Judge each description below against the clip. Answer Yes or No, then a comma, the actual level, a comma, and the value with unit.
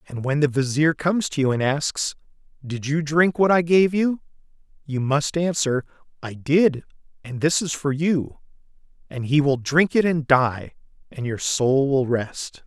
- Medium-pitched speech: Yes, medium, 145 Hz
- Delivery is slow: No, average, 180 wpm